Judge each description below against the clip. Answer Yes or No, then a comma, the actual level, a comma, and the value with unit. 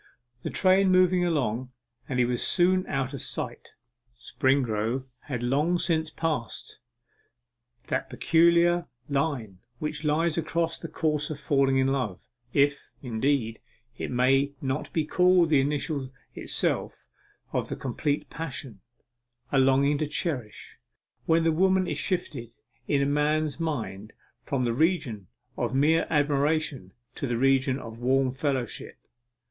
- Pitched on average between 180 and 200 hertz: No, medium, 140 Hz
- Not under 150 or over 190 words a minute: No, slow, 135 wpm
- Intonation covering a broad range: No, average, 3.9 semitones